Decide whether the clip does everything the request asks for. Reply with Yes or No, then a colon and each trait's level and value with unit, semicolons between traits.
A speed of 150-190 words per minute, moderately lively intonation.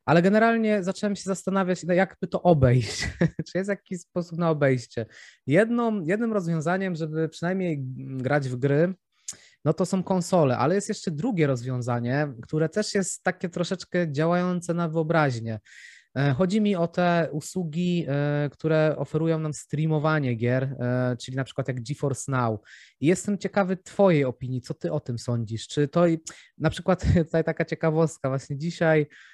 Yes: average, 155 wpm; average, 4.7 semitones